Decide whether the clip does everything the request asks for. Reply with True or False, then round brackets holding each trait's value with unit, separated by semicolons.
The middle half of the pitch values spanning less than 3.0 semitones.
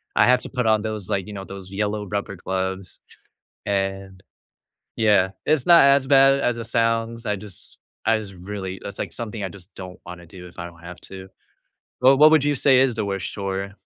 False (3.5 semitones)